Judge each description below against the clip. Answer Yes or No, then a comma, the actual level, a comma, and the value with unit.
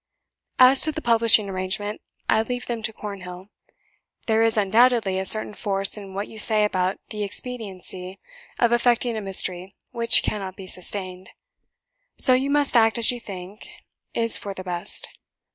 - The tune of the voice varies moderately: Yes, average, 3.5 semitones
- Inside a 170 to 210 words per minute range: No, average, 160 wpm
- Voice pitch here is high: Yes, high, 210 Hz